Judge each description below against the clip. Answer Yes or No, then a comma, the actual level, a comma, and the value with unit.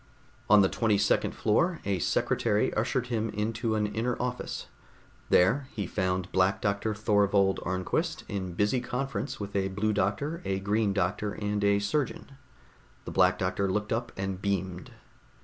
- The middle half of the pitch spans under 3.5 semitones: Yes, narrow, 2.6 semitones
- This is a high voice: No, low, 105 Hz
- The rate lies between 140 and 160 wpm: Yes, average, 155 wpm